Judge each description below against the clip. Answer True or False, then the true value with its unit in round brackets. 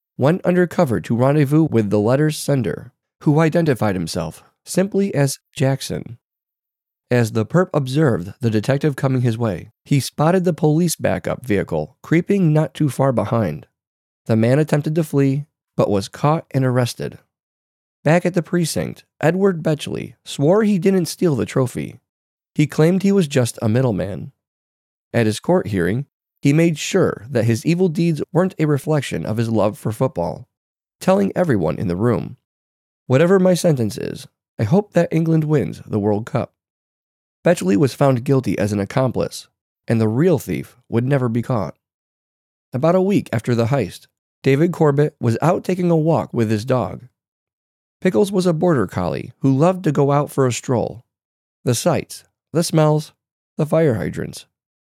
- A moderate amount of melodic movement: False (6.4 semitones)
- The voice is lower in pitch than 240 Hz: True (140 Hz)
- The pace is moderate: True (165 wpm)